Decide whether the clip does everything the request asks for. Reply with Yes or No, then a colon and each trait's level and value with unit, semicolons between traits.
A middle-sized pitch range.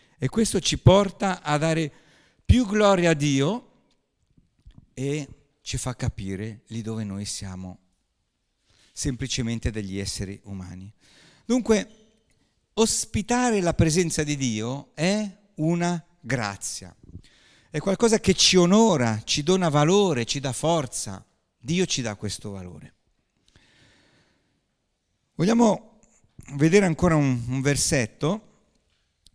No: wide, 8.9 semitones